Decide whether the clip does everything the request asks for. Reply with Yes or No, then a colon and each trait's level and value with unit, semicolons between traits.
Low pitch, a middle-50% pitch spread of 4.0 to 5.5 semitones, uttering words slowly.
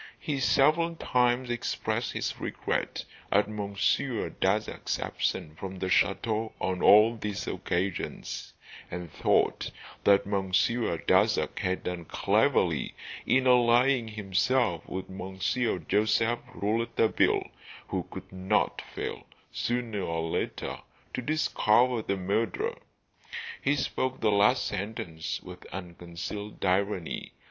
Yes: low, 105 Hz; average, 4.3 semitones; slow, 110 wpm